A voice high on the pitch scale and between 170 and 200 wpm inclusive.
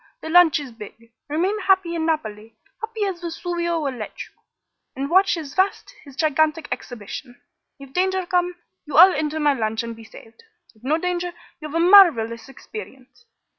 Yes: very high, 315 Hz; average, 175 wpm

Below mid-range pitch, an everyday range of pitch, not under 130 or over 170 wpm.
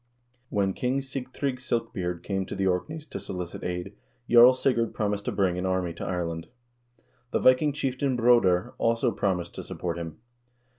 No: low, 100 Hz; wide, 6.0 semitones; average, 160 wpm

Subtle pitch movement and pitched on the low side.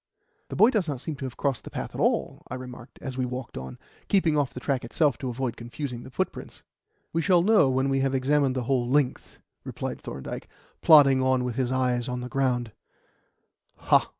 Yes: narrow, 2.3 semitones; low, 130 Hz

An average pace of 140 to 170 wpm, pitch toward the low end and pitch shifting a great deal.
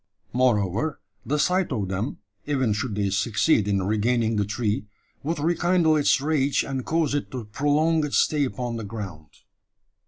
Yes: average, 160 wpm; low, 125 Hz; wide, 6.0 semitones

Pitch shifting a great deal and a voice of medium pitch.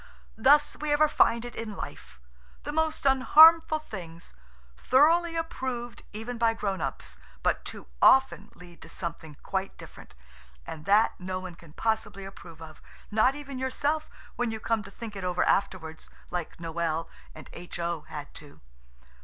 No: wide, 7.7 semitones; high, 210 Hz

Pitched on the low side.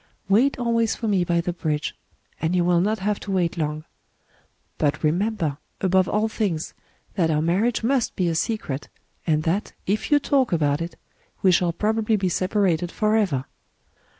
No: medium, 185 Hz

